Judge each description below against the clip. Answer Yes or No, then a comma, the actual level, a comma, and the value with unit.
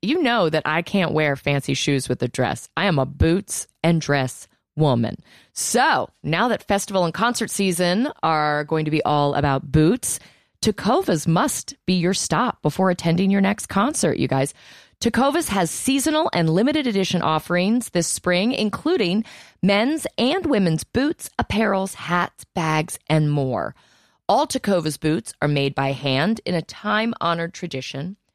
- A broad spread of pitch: Yes, wide, 5.7 semitones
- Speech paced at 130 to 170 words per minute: Yes, average, 160 wpm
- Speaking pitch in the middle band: Yes, medium, 175 Hz